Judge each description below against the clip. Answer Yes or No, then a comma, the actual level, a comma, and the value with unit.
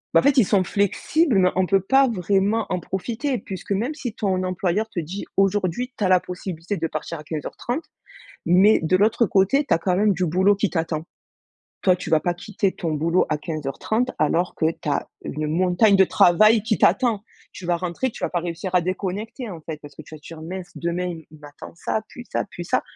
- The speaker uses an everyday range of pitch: Yes, average, 3.8 semitones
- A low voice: No, medium, 185 Hz